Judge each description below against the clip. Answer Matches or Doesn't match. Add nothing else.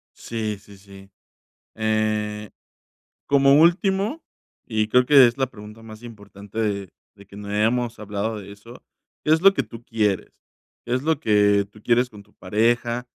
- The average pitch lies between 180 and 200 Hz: Doesn't match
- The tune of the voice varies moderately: Matches